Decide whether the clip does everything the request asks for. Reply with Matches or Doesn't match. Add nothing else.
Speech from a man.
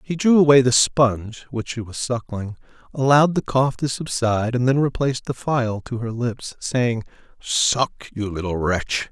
Matches